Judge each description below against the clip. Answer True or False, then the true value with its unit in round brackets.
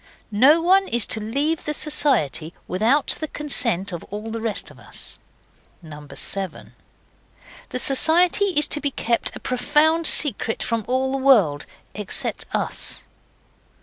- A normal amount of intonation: False (5.8 semitones)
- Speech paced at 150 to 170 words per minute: False (140 wpm)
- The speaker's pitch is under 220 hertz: False (255 Hz)